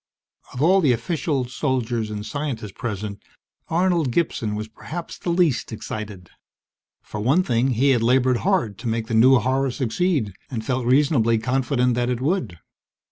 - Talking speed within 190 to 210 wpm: No, average, 160 wpm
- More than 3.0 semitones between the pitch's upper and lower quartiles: Yes, average, 4.3 semitones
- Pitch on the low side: Yes, low, 125 Hz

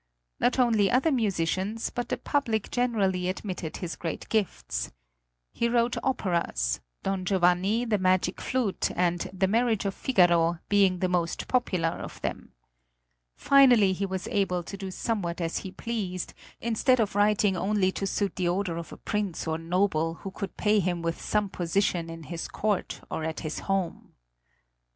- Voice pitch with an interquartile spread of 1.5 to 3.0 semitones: No, average, 3.5 semitones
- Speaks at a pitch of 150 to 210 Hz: Yes, high, 190 Hz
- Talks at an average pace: Yes, average, 165 wpm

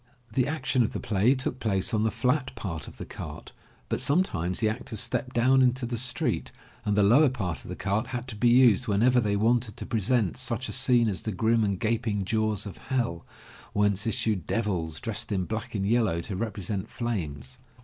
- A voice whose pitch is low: Yes, low, 110 Hz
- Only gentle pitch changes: No, average, 3.5 semitones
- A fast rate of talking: Yes, fast, 210 wpm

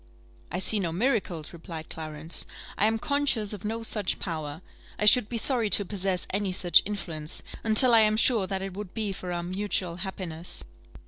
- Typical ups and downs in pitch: Yes, average, 3.8 semitones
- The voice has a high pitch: Yes, high, 195 Hz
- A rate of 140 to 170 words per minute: No, average, 185 wpm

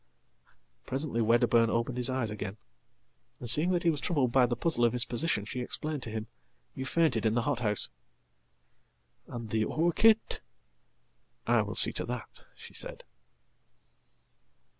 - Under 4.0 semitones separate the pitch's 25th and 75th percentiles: No, average, 5.1 semitones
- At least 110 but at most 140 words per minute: Yes, slow, 135 wpm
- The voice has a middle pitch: No, low, 120 Hz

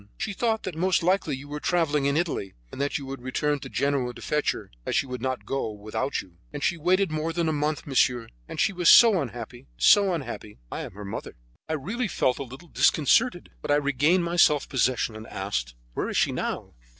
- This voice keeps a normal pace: No, fast, 225 wpm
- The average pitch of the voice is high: No, medium, 145 Hz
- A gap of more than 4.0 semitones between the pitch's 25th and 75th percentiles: Yes, wide, 5.4 semitones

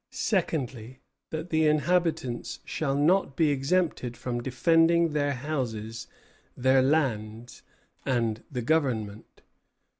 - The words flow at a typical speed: No, slow, 100 wpm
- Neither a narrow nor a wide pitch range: Yes, average, 4.8 semitones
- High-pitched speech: No, low, 135 Hz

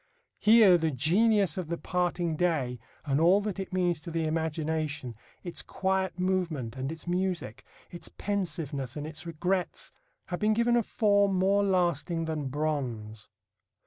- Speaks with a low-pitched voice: No, medium, 170 Hz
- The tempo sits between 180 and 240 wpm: No, average, 150 wpm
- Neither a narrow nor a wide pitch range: Yes, average, 3.8 semitones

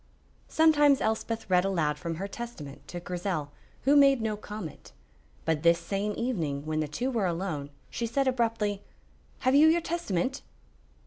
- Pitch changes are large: Yes, wide, 6.9 semitones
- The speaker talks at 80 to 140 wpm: No, average, 155 wpm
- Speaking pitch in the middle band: No, high, 205 Hz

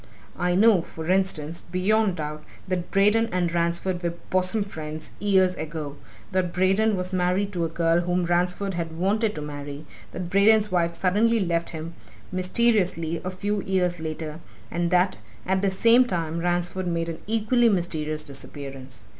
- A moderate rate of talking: Yes, average, 160 wpm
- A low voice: No, medium, 180 Hz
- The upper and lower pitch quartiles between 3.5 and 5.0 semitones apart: No, average, 2.7 semitones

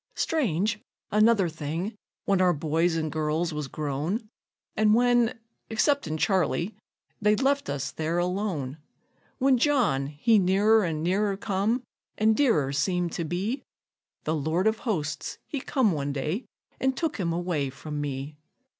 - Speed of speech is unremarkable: Yes, average, 145 wpm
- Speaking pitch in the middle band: Yes, medium, 180 Hz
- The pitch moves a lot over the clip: Yes, wide, 6.1 semitones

